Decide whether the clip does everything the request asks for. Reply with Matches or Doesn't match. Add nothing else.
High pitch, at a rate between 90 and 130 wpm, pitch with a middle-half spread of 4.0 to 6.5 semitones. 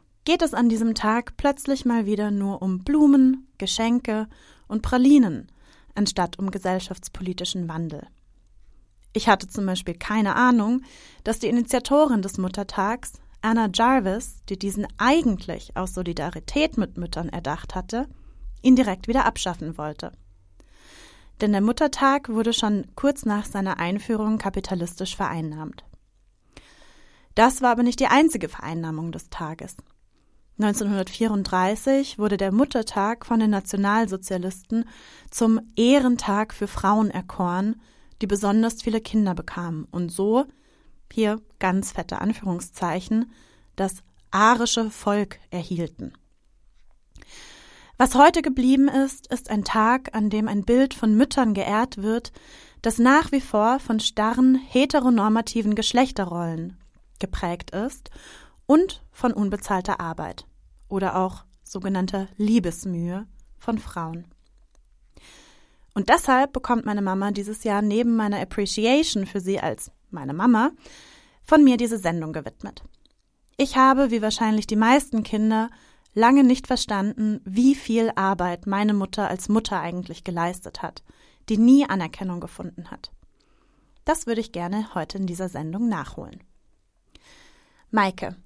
Matches